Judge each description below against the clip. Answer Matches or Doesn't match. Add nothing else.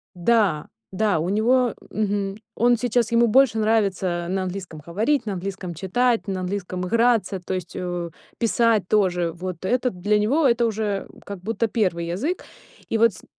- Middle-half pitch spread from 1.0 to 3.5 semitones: Doesn't match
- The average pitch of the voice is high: Matches